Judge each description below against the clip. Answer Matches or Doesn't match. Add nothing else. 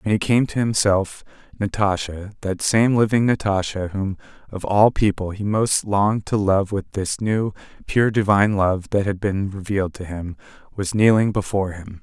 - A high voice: Doesn't match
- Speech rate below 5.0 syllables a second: Matches